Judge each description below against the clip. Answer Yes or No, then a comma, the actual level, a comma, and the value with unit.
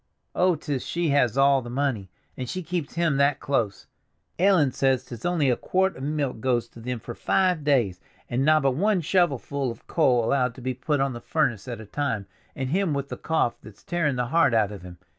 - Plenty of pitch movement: No, average, 4.4 semitones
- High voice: No, low, 135 Hz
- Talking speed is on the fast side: Yes, fast, 215 wpm